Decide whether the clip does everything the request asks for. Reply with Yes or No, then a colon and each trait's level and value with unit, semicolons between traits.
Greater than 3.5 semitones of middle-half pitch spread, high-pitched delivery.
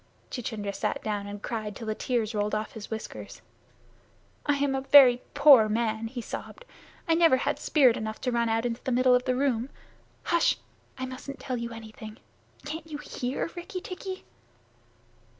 Yes: average, 4.2 semitones; high, 245 Hz